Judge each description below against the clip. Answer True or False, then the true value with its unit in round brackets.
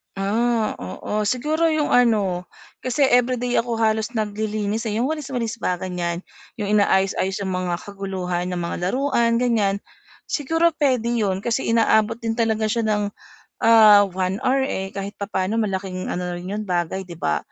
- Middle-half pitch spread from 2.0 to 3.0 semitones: False (3.7 semitones)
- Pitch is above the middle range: True (215 Hz)